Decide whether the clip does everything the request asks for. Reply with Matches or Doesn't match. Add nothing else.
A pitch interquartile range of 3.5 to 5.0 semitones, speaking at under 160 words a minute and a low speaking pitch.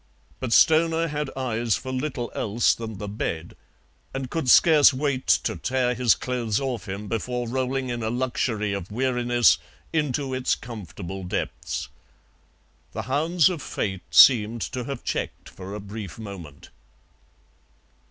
Matches